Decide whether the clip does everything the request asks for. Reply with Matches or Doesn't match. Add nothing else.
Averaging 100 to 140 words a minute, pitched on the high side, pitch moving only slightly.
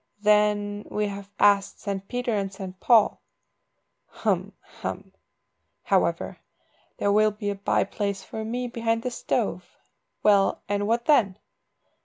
Matches